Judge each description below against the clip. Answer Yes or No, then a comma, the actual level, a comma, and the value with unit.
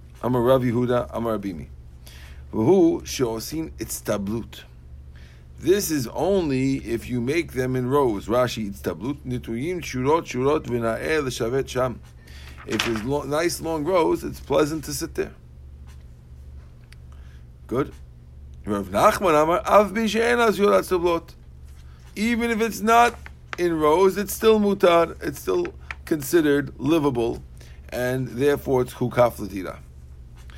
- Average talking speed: No, slow, 130 wpm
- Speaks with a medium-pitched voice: No, low, 120 Hz